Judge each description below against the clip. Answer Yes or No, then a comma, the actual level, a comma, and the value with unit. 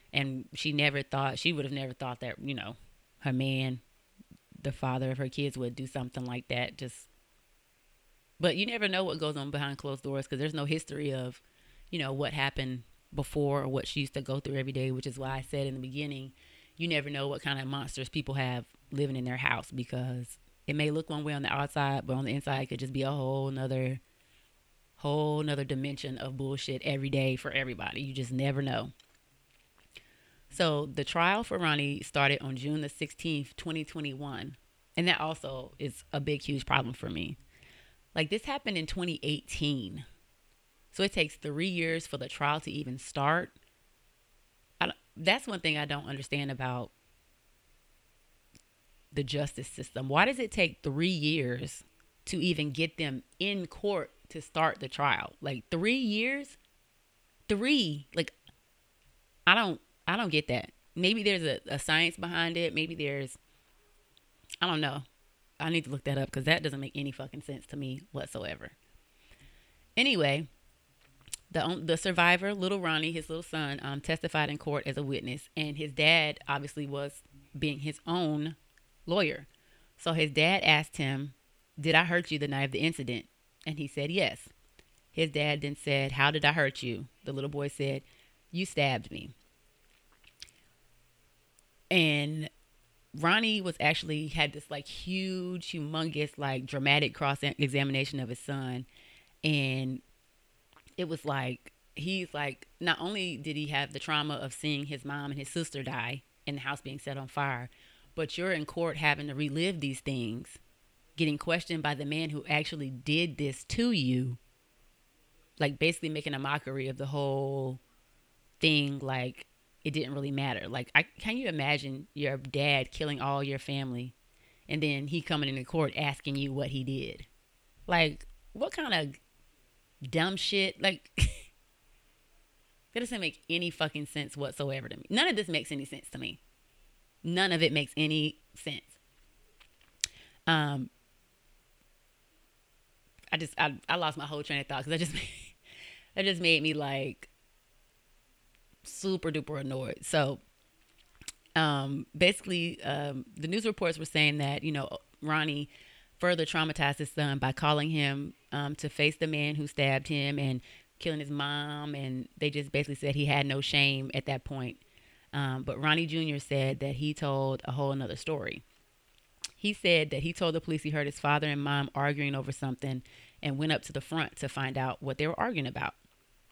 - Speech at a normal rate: Yes, average, 175 wpm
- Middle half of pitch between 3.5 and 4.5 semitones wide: No, average, 2.7 semitones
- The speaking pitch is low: No, medium, 145 Hz